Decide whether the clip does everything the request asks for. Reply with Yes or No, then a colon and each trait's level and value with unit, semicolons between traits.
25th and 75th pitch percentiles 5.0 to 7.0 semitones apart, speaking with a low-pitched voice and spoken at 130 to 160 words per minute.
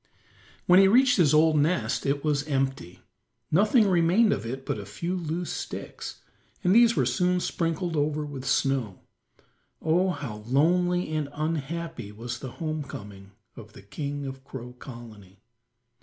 No: average, 5.3 semitones; medium, 150 Hz; average, 155 wpm